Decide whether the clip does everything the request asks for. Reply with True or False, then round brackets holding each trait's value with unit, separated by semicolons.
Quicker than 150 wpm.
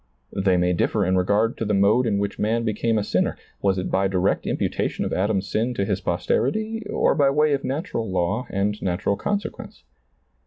True (200 wpm)